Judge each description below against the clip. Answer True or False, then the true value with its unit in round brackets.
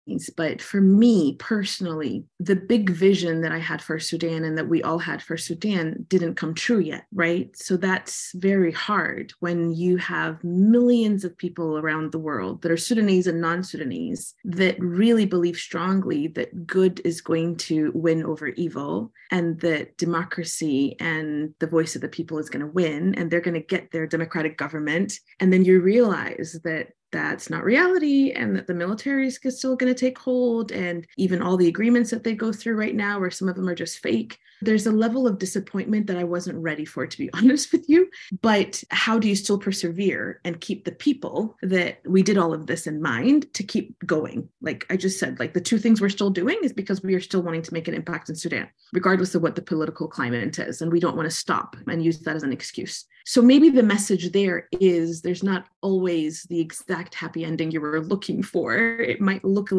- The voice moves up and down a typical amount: True (3.8 semitones)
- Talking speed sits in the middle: False (210 wpm)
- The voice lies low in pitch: False (180 Hz)